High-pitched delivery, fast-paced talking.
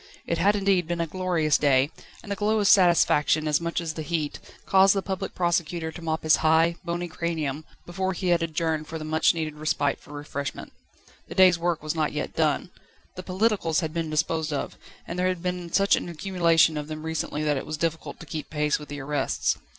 No: medium, 165 Hz; fast, 215 wpm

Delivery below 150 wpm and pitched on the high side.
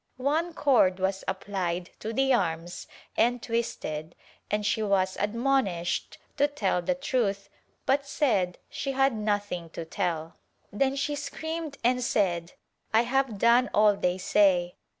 Yes: average, 140 wpm; high, 210 Hz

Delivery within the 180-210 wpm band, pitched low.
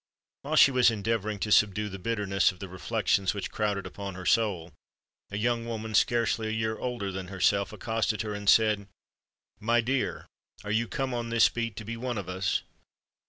Yes: average, 190 wpm; low, 110 Hz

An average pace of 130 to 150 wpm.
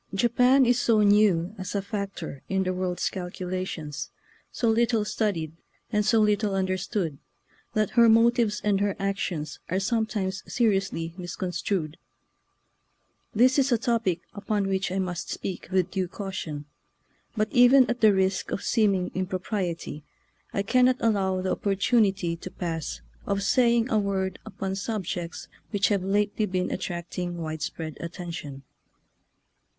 Yes: average, 140 wpm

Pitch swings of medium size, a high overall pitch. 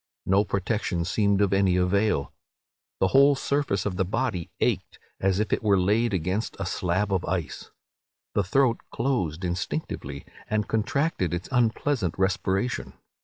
No: average, 3.6 semitones; low, 100 Hz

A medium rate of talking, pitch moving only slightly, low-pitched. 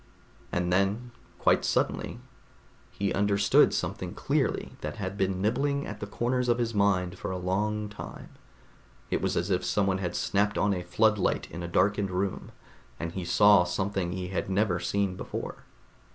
Yes: average, 165 wpm; narrow, 2.3 semitones; low, 100 Hz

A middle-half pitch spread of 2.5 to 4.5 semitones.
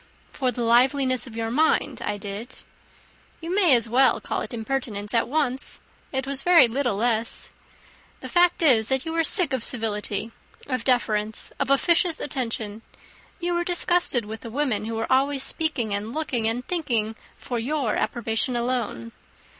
Yes: average, 4.1 semitones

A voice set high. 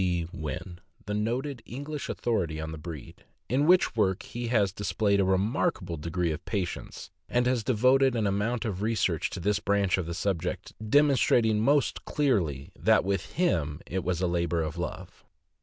No: low, 100 Hz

